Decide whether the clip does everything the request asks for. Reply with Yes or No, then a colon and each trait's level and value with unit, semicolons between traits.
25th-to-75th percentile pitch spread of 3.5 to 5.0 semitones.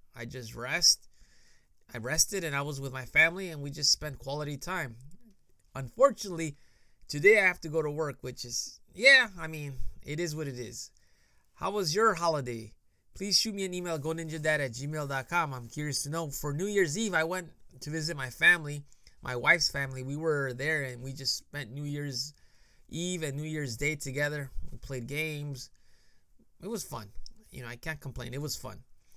Yes: average, 3.8 semitones